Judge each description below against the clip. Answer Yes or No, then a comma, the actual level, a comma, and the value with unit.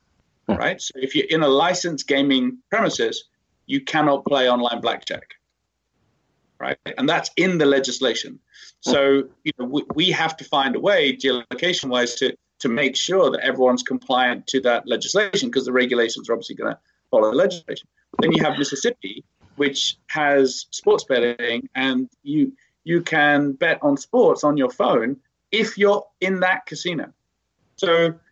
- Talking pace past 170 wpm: No, average, 160 wpm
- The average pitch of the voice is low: No, medium, 155 Hz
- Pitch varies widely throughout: Yes, wide, 7.6 semitones